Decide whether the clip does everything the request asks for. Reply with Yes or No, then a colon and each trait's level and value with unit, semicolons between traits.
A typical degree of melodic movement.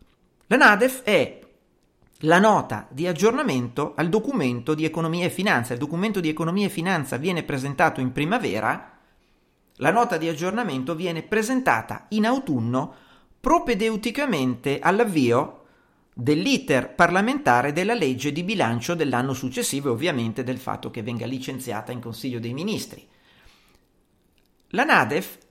No: wide, 8.4 semitones